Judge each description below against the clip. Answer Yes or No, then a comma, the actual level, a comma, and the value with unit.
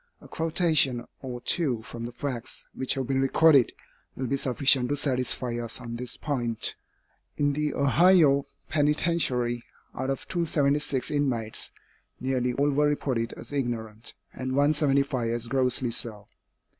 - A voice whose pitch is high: No, low, 135 Hz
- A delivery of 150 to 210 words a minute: No, average, 140 wpm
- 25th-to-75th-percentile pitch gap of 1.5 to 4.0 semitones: Yes, average, 3.1 semitones